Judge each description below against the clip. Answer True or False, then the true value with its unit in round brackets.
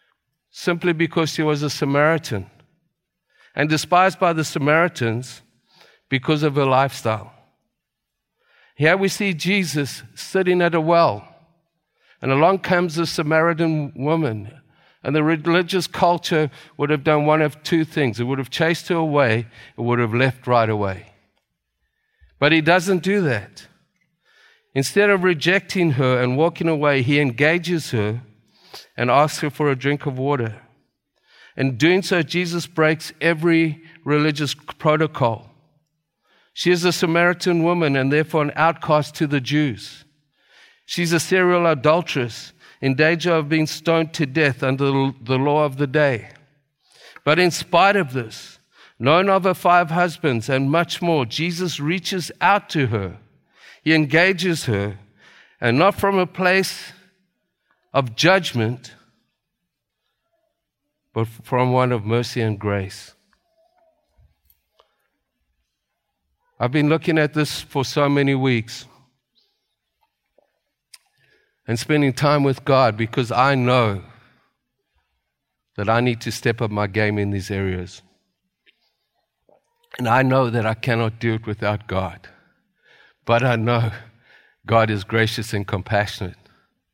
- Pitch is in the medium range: True (145 Hz)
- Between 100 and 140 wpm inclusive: True (135 wpm)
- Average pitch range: False (5.7 semitones)